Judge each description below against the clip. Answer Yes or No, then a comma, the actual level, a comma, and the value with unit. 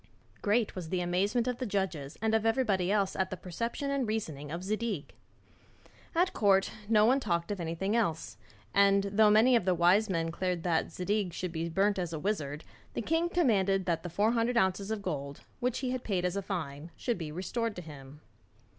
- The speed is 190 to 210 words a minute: Yes, fast, 205 wpm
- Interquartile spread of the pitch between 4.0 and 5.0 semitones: Yes, average, 4.4 semitones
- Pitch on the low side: No, high, 195 Hz